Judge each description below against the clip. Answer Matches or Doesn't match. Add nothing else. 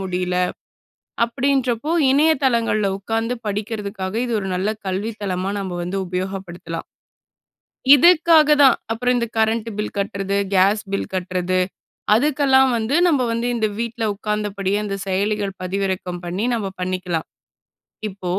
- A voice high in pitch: Matches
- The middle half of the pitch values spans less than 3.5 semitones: Doesn't match